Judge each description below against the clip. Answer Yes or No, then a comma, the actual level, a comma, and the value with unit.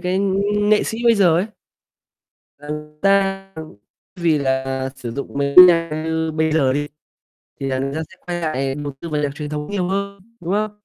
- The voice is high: No, medium, 160 Hz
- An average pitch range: Yes, average, 4.6 semitones